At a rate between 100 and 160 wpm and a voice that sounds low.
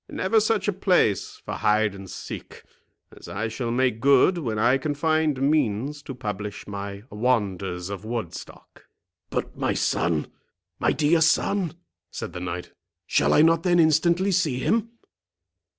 Yes: average, 150 wpm; low, 130 Hz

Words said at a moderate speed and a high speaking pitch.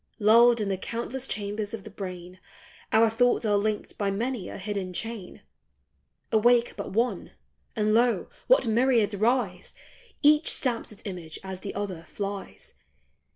Yes: average, 150 wpm; high, 215 Hz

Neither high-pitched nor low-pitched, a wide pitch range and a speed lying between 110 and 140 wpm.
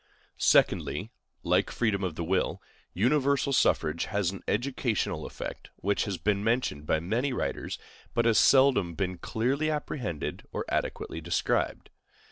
No: low, 105 Hz; wide, 6.2 semitones; slow, 135 wpm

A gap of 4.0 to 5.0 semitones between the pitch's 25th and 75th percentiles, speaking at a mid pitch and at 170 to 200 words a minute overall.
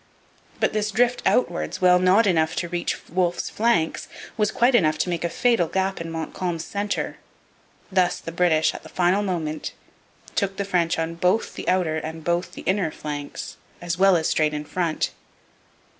No: average, 3.1 semitones; medium, 175 Hz; average, 175 wpm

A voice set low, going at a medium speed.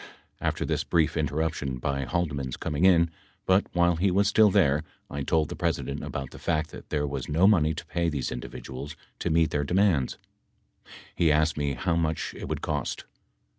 Yes: very low, 80 Hz; average, 190 wpm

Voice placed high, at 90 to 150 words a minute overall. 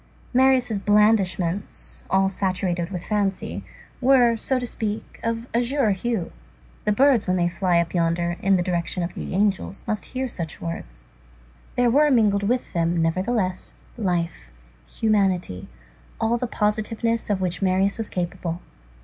Yes: high, 195 Hz; average, 145 wpm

